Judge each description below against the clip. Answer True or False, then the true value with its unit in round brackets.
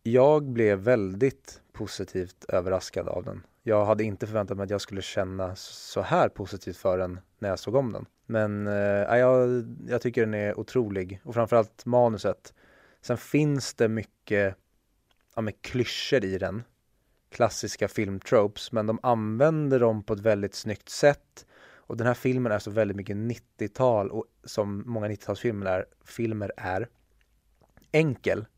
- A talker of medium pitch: False (110 Hz)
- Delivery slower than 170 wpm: True (155 wpm)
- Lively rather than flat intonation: False (3.3 semitones)